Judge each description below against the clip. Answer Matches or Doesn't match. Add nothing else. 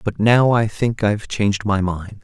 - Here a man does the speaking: Matches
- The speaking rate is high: Matches